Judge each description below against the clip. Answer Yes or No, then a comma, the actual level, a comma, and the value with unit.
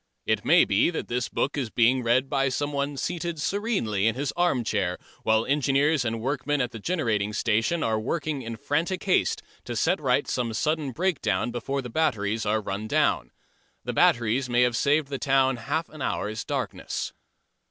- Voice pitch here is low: Yes, low, 130 Hz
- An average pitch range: Yes, average, 4.6 semitones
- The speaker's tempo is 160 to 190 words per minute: Yes, average, 180 wpm